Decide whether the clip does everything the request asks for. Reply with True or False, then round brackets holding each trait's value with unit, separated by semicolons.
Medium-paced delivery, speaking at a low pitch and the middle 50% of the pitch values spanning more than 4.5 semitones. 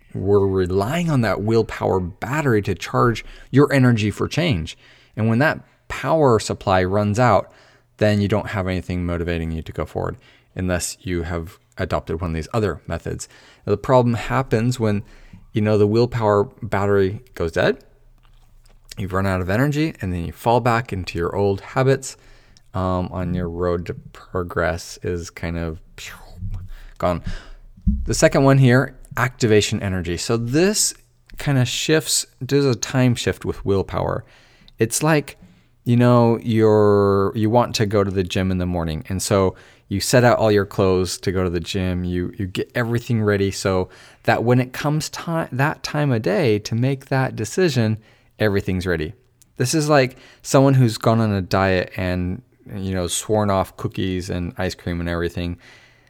True (170 wpm; 105 Hz; 4.9 semitones)